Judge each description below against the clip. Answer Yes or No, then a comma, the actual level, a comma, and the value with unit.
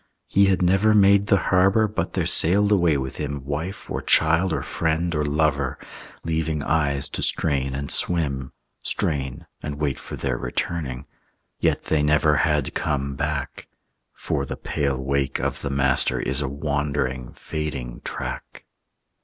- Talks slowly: No, average, 155 wpm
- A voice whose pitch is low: Yes, very low, 75 Hz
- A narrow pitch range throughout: No, average, 3.4 semitones